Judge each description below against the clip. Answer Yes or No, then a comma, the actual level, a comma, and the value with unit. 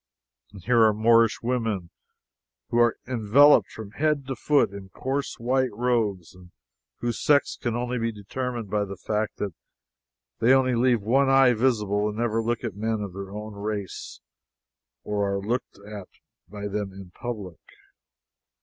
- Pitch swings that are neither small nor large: Yes, average, 3.3 semitones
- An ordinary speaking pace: Yes, average, 160 wpm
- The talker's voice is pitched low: Yes, low, 110 Hz